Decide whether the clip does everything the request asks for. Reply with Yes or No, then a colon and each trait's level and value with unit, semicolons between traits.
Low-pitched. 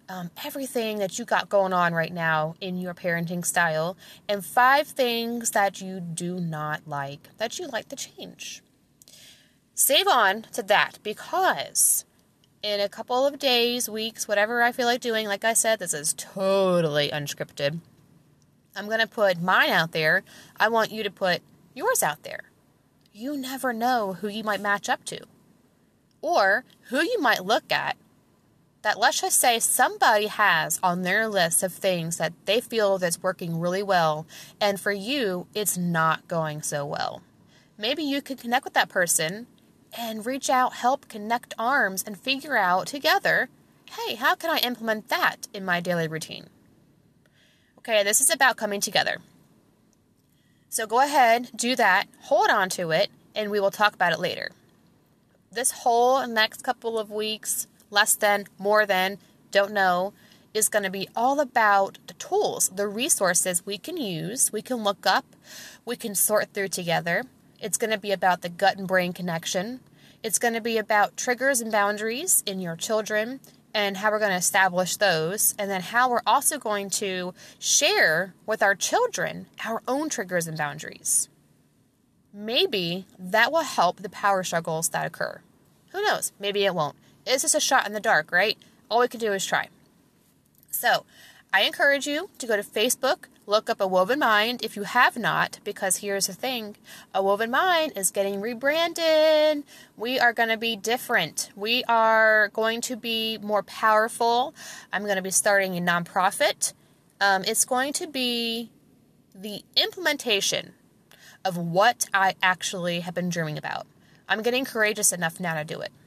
No: high, 210 Hz